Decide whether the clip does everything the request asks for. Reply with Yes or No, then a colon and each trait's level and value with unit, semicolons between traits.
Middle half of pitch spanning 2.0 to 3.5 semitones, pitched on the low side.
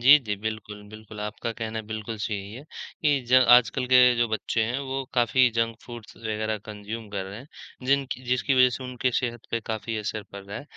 Yes: average, 2.8 semitones; low, 115 Hz